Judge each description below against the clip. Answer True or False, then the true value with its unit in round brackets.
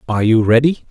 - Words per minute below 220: True (200 wpm)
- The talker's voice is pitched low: True (120 Hz)